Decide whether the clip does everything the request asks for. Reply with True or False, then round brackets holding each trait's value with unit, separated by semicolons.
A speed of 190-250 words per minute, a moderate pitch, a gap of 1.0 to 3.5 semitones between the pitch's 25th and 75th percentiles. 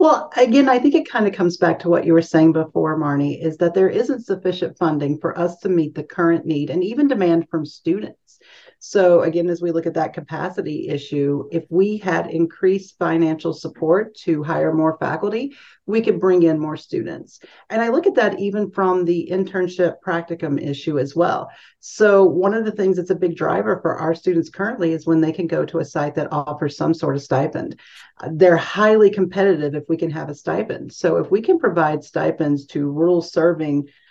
True (205 wpm; 170 Hz; 3.1 semitones)